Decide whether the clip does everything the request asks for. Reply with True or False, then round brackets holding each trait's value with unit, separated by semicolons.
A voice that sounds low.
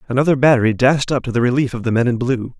True (125 Hz)